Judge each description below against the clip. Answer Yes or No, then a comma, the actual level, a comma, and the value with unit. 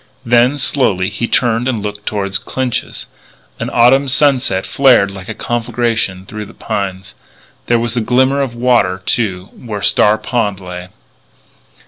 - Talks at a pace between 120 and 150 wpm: Yes, average, 145 wpm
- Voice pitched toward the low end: Yes, low, 115 Hz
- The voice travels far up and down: No, average, 3.9 semitones